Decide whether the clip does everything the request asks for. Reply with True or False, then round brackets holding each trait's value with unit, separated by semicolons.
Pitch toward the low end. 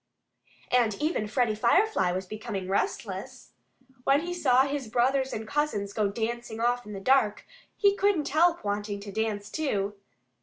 False (235 Hz)